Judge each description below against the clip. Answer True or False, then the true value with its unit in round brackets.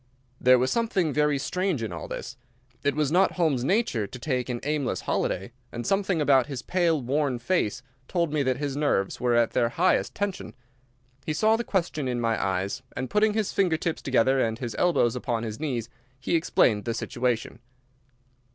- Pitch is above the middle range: False (135 Hz)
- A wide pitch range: True (6.0 semitones)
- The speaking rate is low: False (190 wpm)